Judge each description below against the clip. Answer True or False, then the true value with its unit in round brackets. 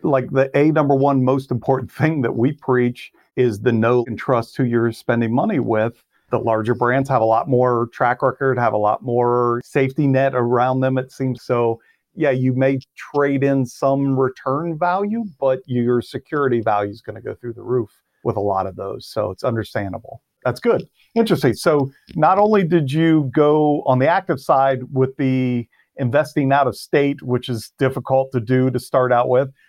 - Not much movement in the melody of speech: True (2.2 semitones)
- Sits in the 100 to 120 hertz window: False (130 Hz)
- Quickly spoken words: False (195 wpm)